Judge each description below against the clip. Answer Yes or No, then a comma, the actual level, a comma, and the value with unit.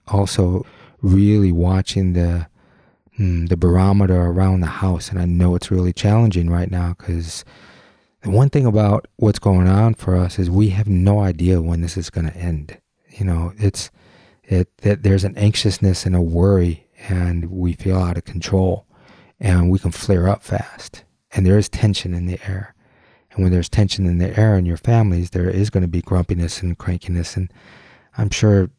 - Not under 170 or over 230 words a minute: Yes, average, 190 wpm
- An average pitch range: No, narrow, 2.3 semitones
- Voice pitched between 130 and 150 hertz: No, very low, 95 Hz